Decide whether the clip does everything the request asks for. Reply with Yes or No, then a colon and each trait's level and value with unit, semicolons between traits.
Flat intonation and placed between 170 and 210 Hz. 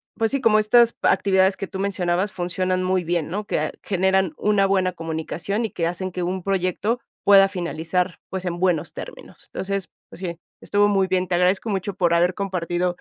Yes: narrow, 2.0 semitones; medium, 185 Hz